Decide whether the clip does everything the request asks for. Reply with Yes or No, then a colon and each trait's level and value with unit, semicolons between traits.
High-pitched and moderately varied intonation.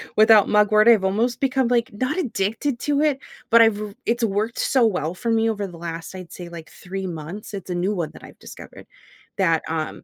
Yes: high, 210 Hz; average, 4.4 semitones